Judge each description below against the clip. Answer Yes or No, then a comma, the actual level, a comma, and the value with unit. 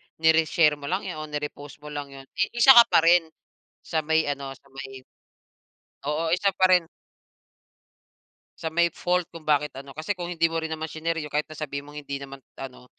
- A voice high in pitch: No, medium, 155 Hz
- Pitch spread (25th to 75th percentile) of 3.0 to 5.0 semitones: No, narrow, 2.6 semitones